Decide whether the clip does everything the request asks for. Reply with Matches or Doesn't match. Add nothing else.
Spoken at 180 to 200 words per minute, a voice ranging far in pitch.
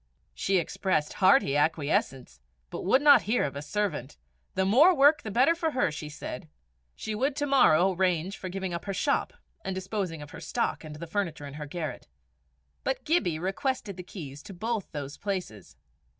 Matches